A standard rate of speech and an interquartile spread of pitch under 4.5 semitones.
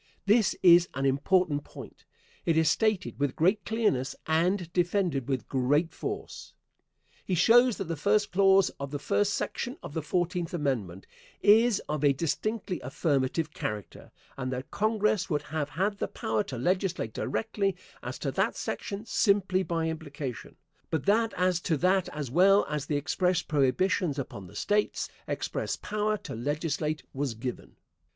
No: average, 160 wpm; wide, 5.6 semitones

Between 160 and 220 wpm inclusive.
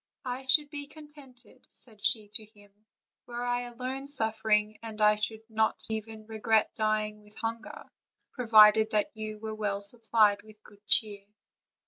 No: average, 150 wpm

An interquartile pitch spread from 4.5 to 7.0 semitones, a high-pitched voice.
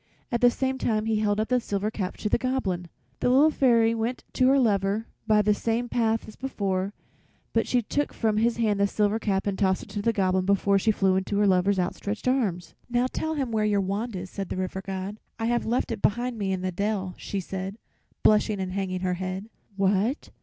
No: average, 3.2 semitones; high, 210 Hz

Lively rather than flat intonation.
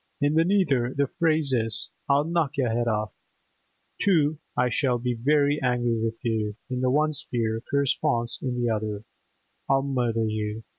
No: average, 4.0 semitones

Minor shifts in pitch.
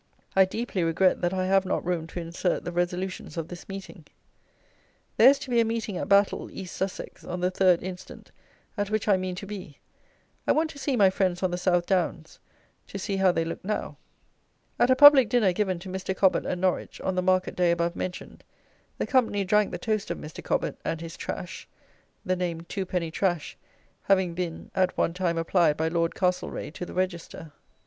Yes: narrow, 2.0 semitones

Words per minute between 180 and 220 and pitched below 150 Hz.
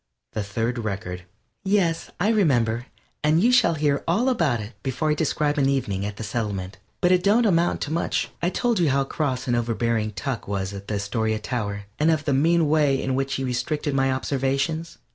Yes: fast, 205 wpm; low, 135 Hz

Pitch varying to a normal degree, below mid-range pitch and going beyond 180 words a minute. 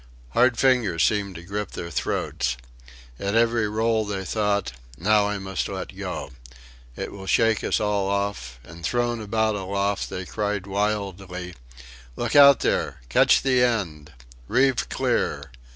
No: average, 3.3 semitones; low, 100 Hz; average, 145 wpm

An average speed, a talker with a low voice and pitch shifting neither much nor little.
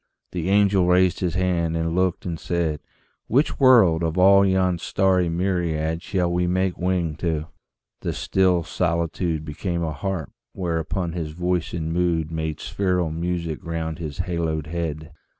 No: average, 150 wpm; very low, 85 Hz; narrow, 2.2 semitones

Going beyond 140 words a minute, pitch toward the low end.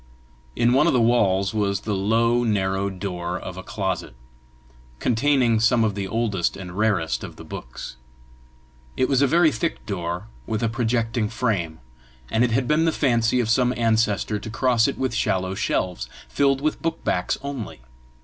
Yes: average, 175 wpm; low, 110 Hz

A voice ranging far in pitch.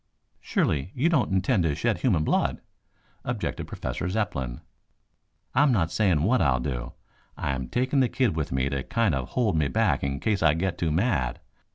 Yes: wide, 8.3 semitones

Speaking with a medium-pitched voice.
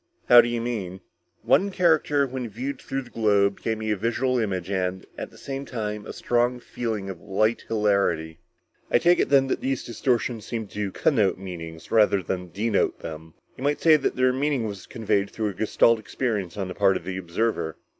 No: low, 110 Hz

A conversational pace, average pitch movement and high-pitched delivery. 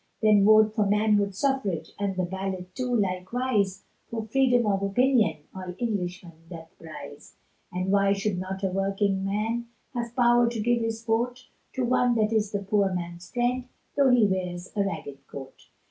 Yes: average, 170 wpm; average, 4.1 semitones; high, 205 Hz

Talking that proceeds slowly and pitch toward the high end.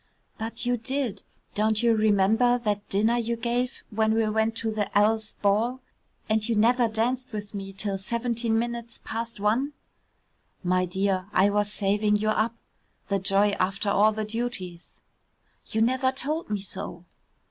No: average, 160 wpm; high, 220 Hz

